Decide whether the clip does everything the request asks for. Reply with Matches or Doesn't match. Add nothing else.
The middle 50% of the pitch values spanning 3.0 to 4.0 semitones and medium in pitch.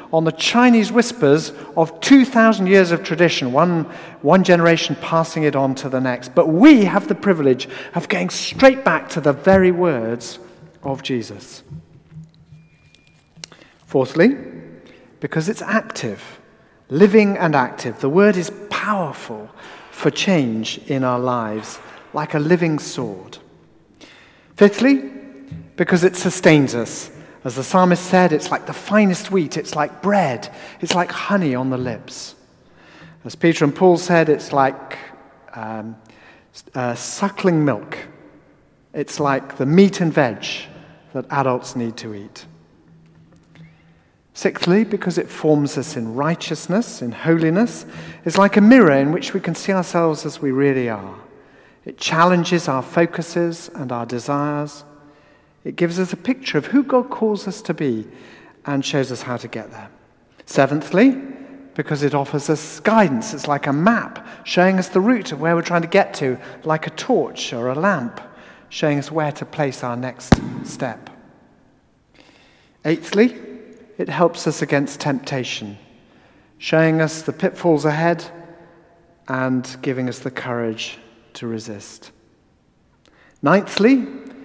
Doesn't match